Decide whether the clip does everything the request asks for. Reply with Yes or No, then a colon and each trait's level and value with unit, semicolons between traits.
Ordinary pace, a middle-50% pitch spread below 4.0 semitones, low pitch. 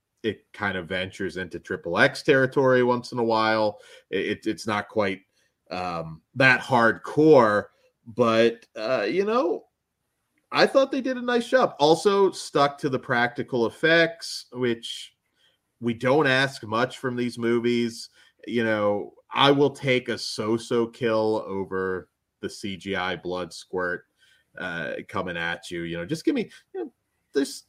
No: average, 150 wpm; average, 4.4 semitones; low, 120 Hz